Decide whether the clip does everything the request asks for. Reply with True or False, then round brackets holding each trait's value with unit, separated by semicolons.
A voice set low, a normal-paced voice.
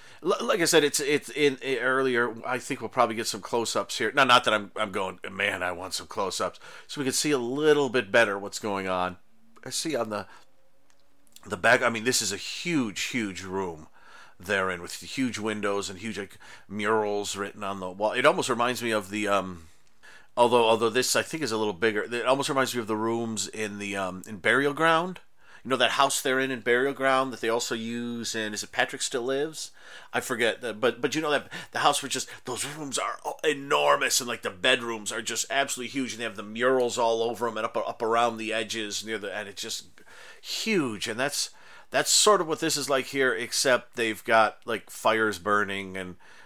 False (115 Hz; 225 wpm)